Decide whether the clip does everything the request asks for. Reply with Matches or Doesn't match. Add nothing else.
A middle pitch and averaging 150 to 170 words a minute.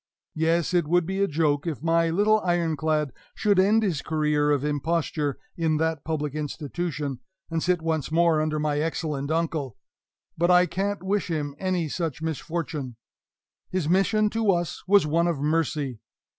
Matches